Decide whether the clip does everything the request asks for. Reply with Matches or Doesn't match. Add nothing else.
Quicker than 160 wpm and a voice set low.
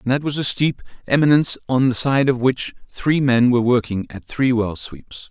Matches